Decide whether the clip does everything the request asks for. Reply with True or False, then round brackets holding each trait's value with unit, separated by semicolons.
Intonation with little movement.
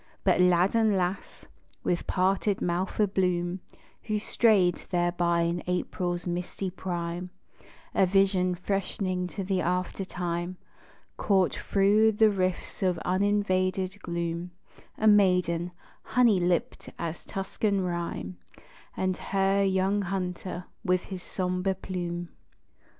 True (1.8 semitones)